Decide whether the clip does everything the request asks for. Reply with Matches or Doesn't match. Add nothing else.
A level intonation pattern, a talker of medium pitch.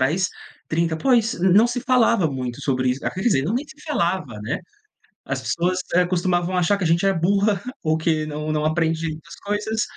Doesn't match